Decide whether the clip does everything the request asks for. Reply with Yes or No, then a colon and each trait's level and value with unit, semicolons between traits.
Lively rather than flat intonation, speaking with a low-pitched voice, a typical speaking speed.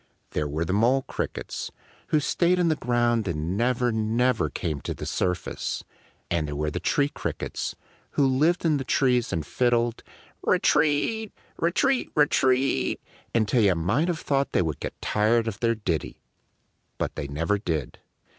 Yes: wide, 7.7 semitones; low, 120 Hz; average, 170 wpm